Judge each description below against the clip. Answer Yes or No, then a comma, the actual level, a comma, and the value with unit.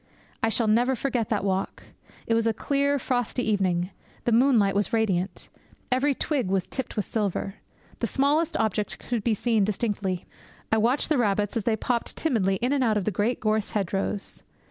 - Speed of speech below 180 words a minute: No, average, 185 wpm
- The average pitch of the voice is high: Yes, high, 220 Hz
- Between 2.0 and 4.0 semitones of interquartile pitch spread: Yes, average, 3.7 semitones